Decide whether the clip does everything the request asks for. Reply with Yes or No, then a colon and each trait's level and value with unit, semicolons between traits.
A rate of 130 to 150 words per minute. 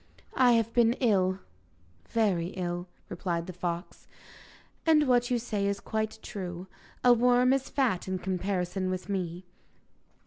Yes: average, 140 wpm